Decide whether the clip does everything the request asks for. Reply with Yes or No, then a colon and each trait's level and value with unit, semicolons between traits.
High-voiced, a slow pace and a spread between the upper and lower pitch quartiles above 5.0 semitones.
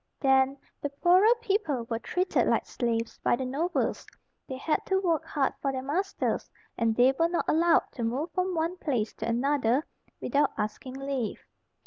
No: very high, 275 Hz; average, 170 wpm; wide, 5.4 semitones